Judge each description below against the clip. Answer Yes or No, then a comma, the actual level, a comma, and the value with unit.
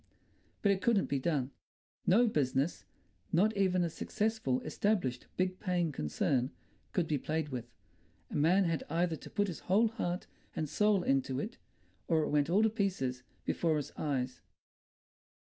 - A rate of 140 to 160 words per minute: Yes, average, 150 wpm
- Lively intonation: Yes, wide, 6.4 semitones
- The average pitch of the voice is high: No, medium, 165 Hz